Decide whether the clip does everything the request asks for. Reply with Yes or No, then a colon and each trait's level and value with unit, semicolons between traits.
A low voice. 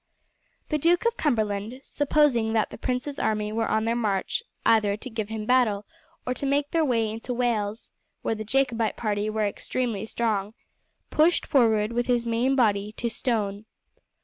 No: high, 225 Hz